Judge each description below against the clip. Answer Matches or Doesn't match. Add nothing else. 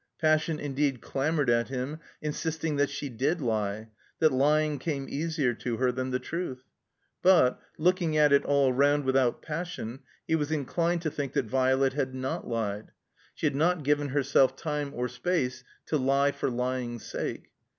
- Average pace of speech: Matches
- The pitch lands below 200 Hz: Matches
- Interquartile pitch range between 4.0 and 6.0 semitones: Doesn't match